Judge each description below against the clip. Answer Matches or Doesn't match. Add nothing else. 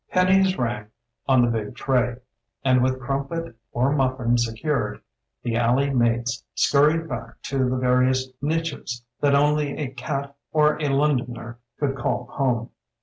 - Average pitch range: Matches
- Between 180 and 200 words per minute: Doesn't match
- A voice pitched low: Matches